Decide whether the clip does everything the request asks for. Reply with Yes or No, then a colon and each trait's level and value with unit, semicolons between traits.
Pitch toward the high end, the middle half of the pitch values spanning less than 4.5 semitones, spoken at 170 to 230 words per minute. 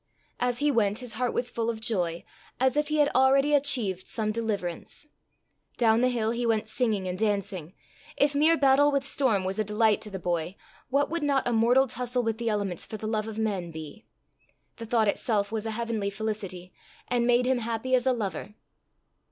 Yes: high, 225 Hz; average, 3.6 semitones; average, 200 wpm